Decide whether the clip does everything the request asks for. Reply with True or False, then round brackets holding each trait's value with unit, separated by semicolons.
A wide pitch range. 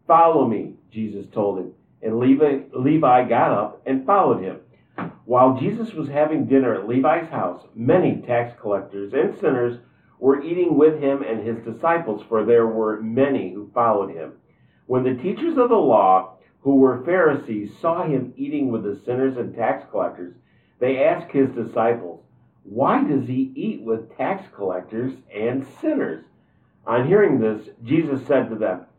False (4.1 semitones)